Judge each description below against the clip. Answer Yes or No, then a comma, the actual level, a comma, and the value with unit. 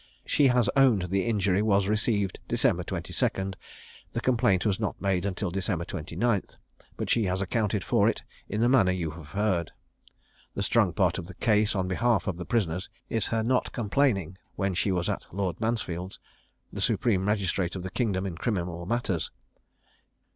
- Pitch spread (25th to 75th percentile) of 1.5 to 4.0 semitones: Yes, average, 3.3 semitones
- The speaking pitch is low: Yes, low, 100 Hz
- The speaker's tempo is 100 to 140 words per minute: No, average, 175 wpm